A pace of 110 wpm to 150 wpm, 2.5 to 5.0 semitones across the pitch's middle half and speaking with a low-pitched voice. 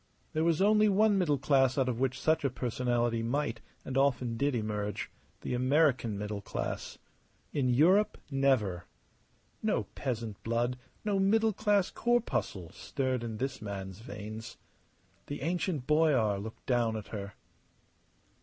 No: average, 140 wpm; wide, 5.6 semitones; low, 130 Hz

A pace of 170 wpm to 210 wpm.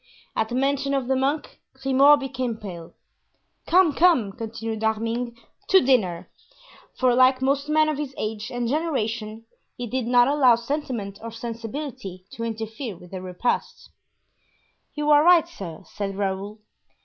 No: average, 150 wpm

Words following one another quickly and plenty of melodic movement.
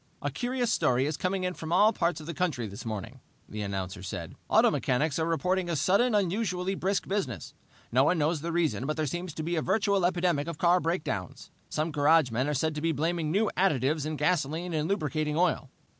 No: fast, 210 wpm; average, 4.1 semitones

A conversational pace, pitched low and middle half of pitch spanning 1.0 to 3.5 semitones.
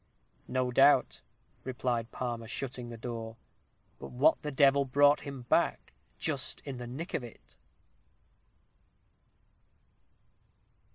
No: slow, 110 wpm; low, 125 Hz; narrow, 2.6 semitones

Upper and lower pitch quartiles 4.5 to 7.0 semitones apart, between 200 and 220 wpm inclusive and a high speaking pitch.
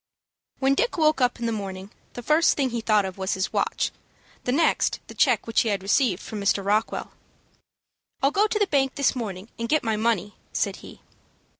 Yes: average, 5.3 semitones; fast, 205 wpm; high, 230 Hz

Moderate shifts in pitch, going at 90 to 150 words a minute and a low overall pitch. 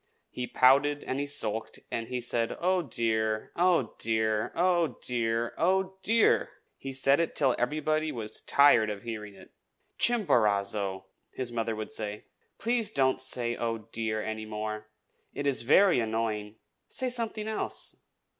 No: wide, 5.9 semitones; average, 145 wpm; low, 120 Hz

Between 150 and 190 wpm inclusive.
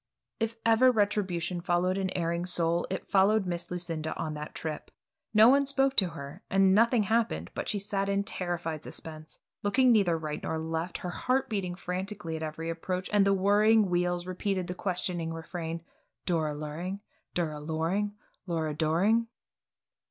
Yes: average, 165 wpm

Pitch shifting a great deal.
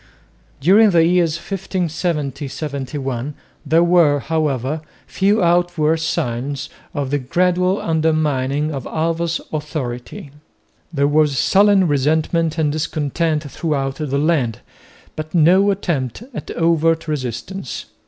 No: average, 3.3 semitones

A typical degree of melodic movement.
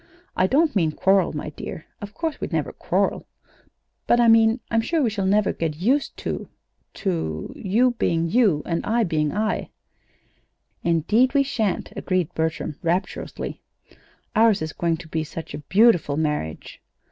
No: wide, 5.8 semitones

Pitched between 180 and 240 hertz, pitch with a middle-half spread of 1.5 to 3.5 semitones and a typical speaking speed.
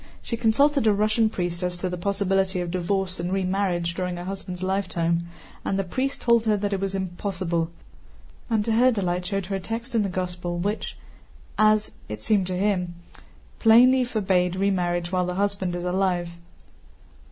Yes: high, 190 Hz; average, 2.8 semitones; average, 175 wpm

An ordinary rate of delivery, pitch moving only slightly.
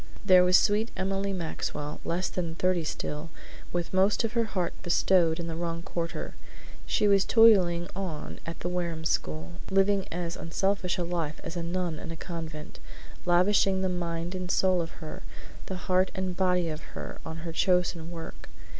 Yes: average, 175 wpm; narrow, 2.2 semitones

